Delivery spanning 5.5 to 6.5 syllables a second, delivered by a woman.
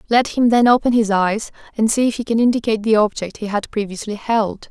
Yes: 5.8 syllables/s; female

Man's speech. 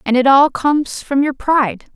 No: female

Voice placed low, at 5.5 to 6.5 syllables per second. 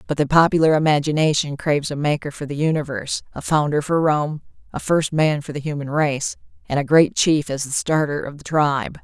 No: medium, 150 Hz; 5.6 syllables/s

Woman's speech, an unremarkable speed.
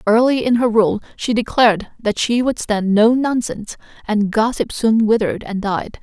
Yes: female; average, 180 wpm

